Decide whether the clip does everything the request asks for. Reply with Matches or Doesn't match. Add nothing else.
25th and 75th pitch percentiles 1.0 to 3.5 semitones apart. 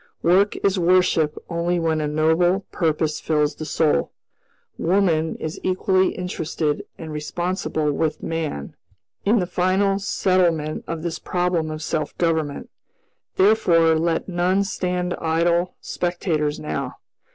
Matches